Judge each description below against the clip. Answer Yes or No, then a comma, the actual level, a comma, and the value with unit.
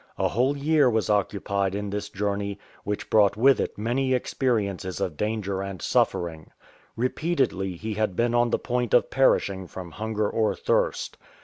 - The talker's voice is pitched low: Yes, low, 105 Hz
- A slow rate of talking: No, average, 165 wpm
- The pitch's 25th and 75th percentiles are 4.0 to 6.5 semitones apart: No, average, 3.6 semitones